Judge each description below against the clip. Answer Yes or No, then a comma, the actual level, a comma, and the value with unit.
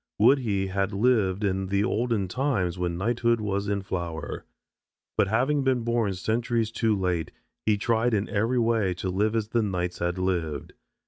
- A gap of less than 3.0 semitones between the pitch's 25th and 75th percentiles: No, average, 3.8 semitones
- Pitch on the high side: No, low, 105 Hz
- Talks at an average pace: Yes, average, 175 wpm